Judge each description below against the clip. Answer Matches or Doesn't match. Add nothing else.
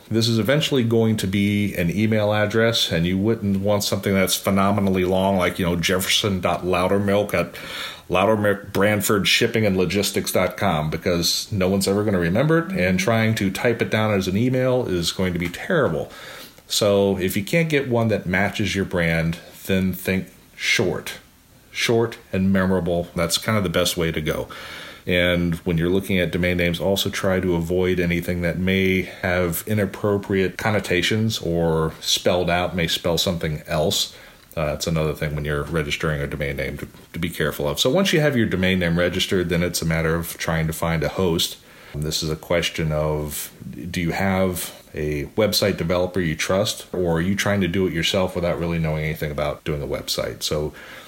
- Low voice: Matches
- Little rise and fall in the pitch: Doesn't match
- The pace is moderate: Matches